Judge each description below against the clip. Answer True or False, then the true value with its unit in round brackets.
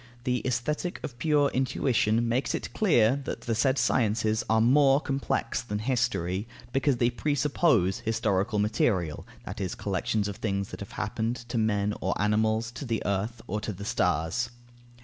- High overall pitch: False (115 Hz)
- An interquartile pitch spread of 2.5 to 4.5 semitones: True (3.6 semitones)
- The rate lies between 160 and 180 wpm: True (165 wpm)